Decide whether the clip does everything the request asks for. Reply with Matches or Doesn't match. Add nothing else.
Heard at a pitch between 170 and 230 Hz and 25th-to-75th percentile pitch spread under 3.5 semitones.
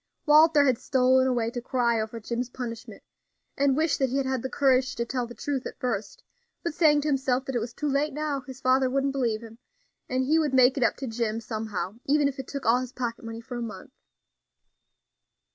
Doesn't match